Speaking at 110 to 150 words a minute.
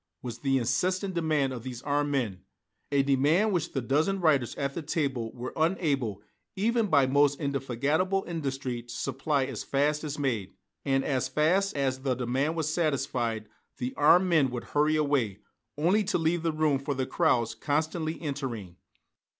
No: average, 165 wpm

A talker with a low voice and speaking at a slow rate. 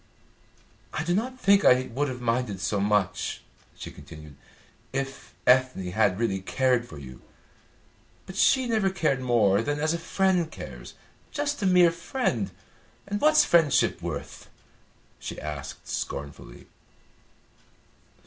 Yes: low, 130 Hz; slow, 130 wpm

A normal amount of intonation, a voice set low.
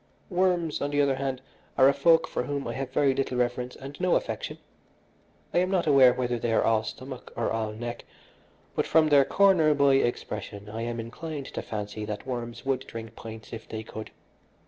Yes: average, 4.0 semitones; low, 130 Hz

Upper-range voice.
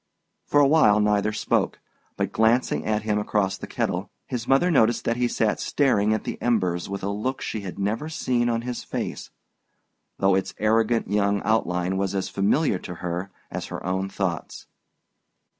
No: low, 105 Hz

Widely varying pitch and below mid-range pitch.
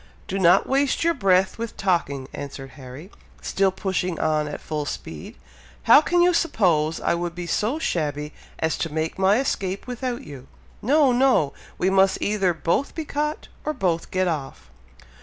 No: wide, 7.7 semitones; medium, 185 Hz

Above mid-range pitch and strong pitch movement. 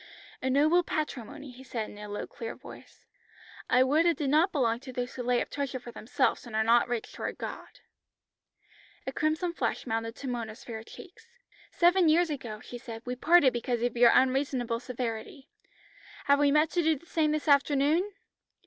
No: very high, 260 Hz; average, 4.2 semitones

